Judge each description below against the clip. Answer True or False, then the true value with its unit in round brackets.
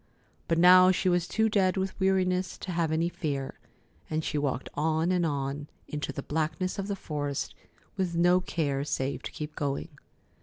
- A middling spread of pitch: True (3.8 semitones)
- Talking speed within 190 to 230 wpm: False (180 wpm)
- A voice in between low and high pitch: True (165 Hz)